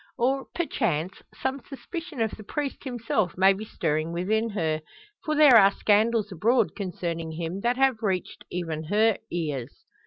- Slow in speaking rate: No, average, 155 wpm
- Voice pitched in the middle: No, high, 210 Hz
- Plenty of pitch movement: Yes, wide, 6.0 semitones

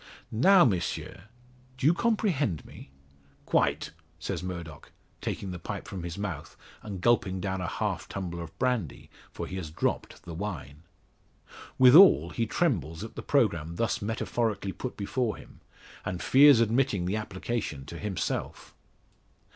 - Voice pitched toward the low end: Yes, low, 100 Hz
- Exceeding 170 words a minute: No, average, 145 wpm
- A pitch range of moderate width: No, wide, 5.7 semitones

